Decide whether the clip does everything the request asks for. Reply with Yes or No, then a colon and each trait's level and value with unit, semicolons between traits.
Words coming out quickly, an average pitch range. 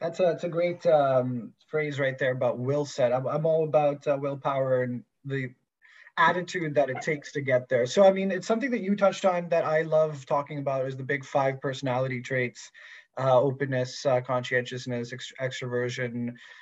No: average, 190 wpm; average, 3.6 semitones